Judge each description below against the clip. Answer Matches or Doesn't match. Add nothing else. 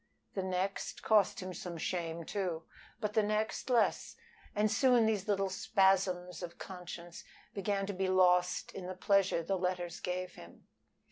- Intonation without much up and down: Matches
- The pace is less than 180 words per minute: Matches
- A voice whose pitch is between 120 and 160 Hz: Doesn't match